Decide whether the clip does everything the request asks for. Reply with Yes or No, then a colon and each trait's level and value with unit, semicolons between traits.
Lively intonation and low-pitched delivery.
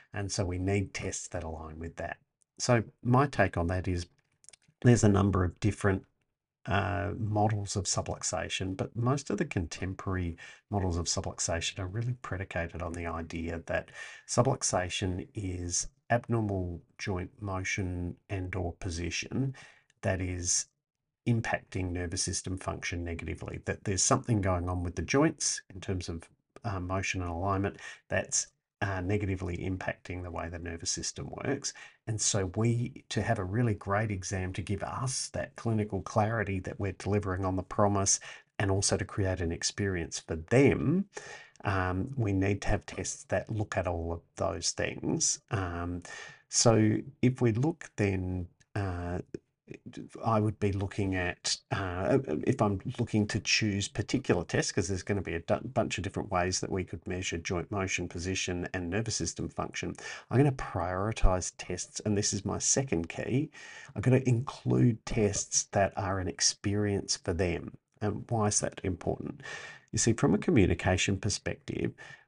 No: average, 3.1 semitones; low, 100 Hz